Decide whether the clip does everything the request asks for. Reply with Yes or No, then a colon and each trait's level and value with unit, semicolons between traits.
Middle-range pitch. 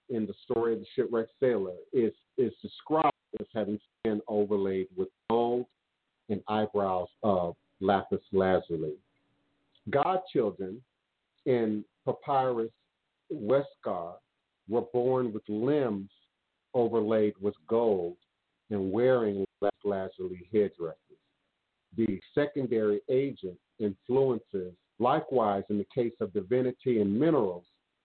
No: low, 105 Hz